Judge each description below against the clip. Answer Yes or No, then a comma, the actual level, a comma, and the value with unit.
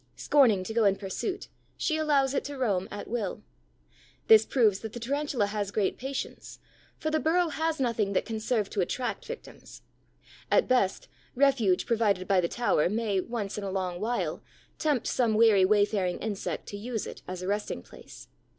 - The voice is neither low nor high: No, high, 220 Hz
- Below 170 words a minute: No, average, 180 wpm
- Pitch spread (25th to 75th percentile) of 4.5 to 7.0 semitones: Yes, average, 5.1 semitones